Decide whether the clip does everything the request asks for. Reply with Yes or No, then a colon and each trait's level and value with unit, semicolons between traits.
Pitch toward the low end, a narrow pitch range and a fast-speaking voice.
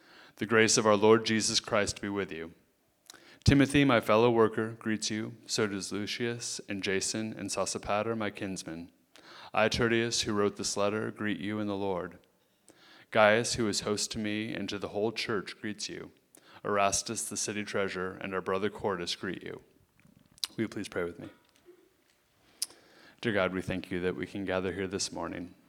No: low, 105 Hz; narrow, 2.3 semitones; average, 180 wpm